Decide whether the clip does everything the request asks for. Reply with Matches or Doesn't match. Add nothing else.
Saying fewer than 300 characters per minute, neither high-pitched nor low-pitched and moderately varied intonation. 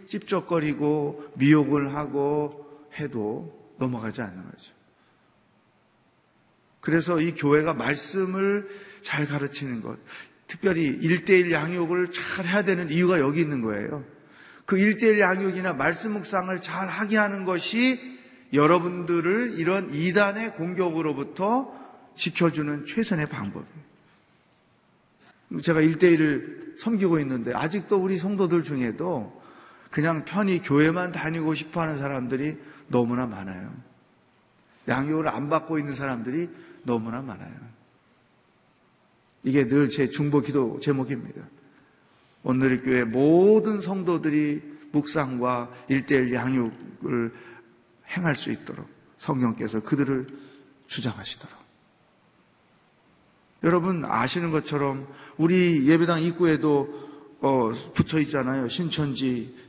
Matches